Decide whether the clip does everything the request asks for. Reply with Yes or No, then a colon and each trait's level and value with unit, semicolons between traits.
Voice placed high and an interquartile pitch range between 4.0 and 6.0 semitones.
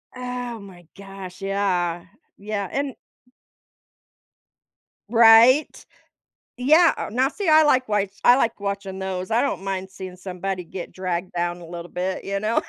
Yes: high, 195 Hz; average, 4.4 semitones